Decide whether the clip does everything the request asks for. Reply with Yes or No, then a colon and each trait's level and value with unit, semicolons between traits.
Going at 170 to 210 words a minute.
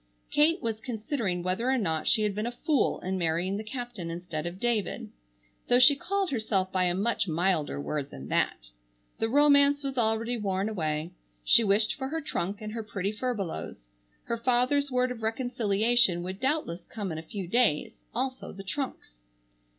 Yes: average, 180 wpm